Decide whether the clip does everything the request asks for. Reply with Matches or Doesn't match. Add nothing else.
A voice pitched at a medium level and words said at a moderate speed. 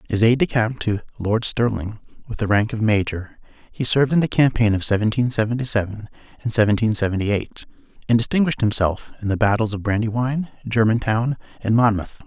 Doesn't match